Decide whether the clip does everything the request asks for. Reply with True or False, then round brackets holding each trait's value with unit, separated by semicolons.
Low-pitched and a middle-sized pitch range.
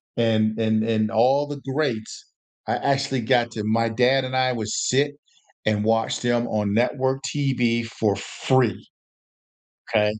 True (115 Hz; 3.1 semitones)